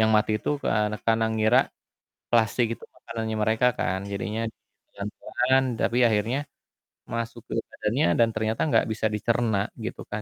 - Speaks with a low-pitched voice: Yes, low, 110 Hz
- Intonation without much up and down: Yes, narrow, 1.5 semitones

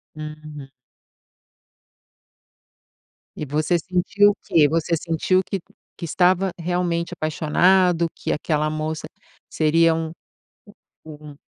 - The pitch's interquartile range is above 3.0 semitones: No, narrow, 2.6 semitones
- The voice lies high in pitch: No, medium, 165 Hz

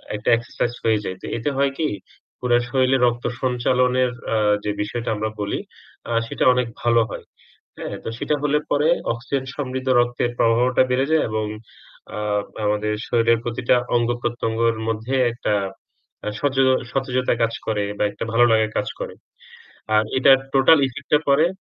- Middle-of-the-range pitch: No, low, 120 Hz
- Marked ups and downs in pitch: No, narrow, 2.4 semitones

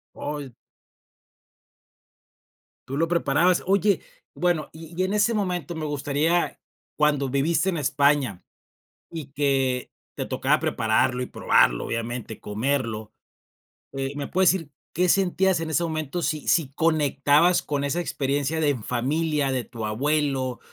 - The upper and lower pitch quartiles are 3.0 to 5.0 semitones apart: Yes, average, 3.8 semitones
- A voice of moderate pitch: Yes, medium, 145 Hz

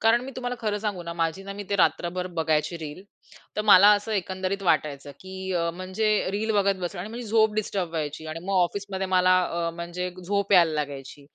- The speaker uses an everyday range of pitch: Yes, average, 3.2 semitones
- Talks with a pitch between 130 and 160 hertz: No, medium, 185 Hz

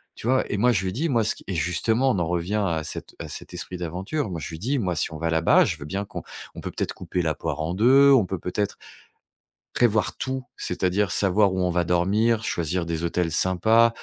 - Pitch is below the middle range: Yes, very low, 95 Hz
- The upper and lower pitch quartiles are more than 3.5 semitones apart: Yes, average, 4.7 semitones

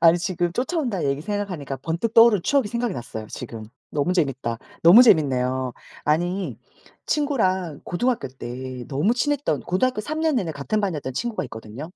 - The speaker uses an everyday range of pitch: No, wide, 8.9 semitones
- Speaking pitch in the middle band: Yes, medium, 175 Hz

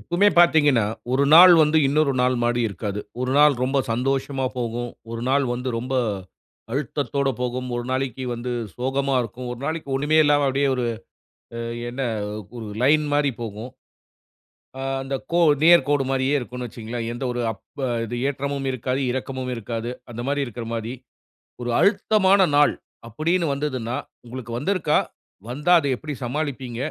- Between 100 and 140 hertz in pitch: Yes, low, 135 Hz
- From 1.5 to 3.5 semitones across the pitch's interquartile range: Yes, average, 3.2 semitones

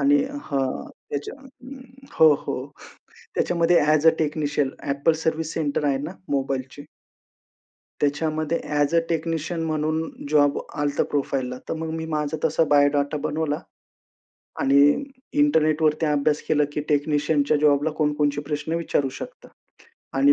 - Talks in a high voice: No, medium, 150 Hz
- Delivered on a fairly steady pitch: Yes, narrow, 1.8 semitones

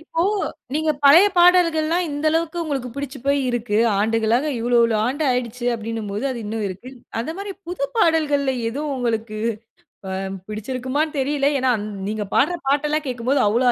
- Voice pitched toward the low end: No, very high, 265 Hz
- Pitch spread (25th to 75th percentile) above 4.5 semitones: Yes, average, 5.1 semitones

